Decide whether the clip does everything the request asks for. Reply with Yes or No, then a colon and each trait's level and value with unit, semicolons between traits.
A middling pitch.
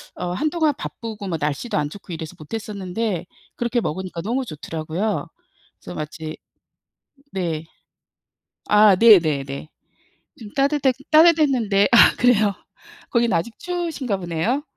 No: high, 205 Hz